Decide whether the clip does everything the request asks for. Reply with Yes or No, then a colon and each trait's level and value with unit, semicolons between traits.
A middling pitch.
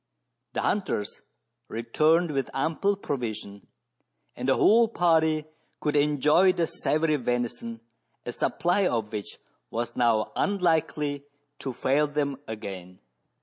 Yes: medium, 145 Hz